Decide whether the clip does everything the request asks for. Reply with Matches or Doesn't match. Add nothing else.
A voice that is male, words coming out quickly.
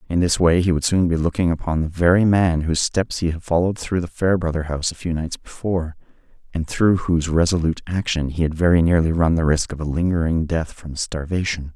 Matches